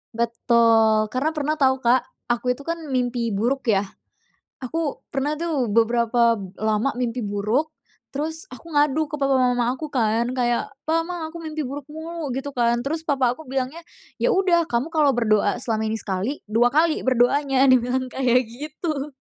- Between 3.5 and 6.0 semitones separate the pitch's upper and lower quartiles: Yes, average, 4.2 semitones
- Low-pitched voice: No, very high, 255 Hz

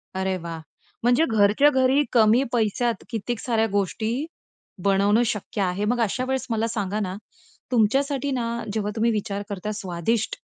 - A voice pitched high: Yes, high, 220 Hz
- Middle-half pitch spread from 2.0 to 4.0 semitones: Yes, average, 3.2 semitones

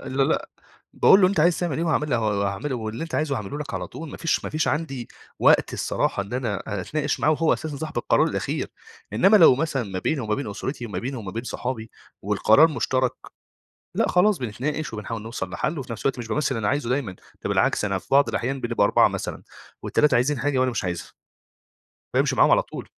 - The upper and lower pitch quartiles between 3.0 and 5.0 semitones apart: No, wide, 5.4 semitones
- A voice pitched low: Yes, low, 130 Hz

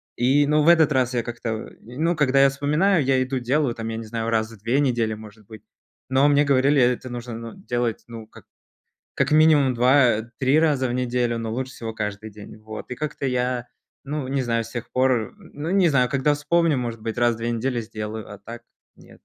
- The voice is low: Yes, low, 125 Hz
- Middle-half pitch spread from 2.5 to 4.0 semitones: Yes, average, 3.6 semitones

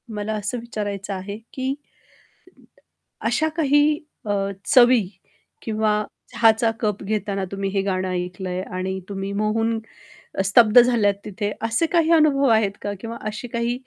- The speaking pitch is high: Yes, high, 215 Hz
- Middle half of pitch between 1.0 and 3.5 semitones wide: Yes, average, 3.2 semitones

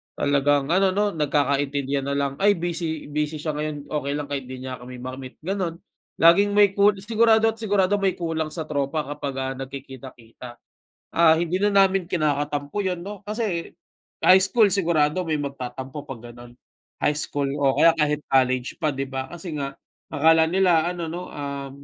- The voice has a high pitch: No, medium, 150 Hz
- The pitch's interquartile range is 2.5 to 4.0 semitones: No, average, 4.8 semitones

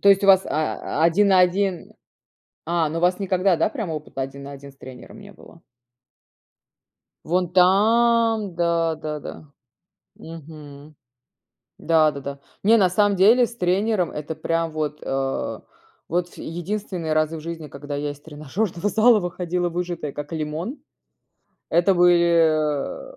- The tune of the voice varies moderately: Yes, average, 3.9 semitones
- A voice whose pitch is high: No, medium, 170 Hz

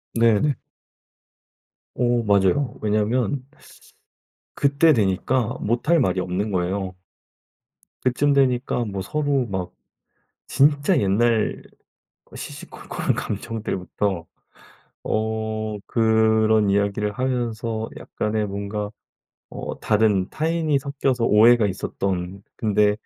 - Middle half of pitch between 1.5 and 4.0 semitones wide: Yes, average, 3.7 semitones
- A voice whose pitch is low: Yes, low, 110 Hz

